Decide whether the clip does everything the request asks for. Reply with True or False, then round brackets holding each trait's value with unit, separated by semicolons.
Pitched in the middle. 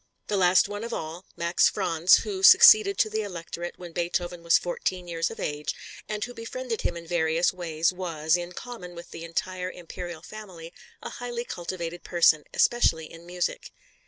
True (175 Hz)